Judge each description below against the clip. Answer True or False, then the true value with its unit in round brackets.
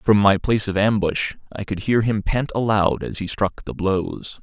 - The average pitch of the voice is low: True (105 Hz)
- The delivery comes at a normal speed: False (215 wpm)